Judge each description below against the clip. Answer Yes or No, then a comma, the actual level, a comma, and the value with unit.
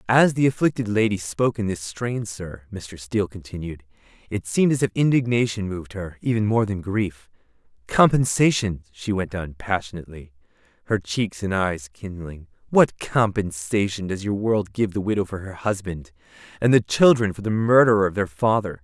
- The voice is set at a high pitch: No, low, 100 Hz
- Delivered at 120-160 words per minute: No, average, 170 wpm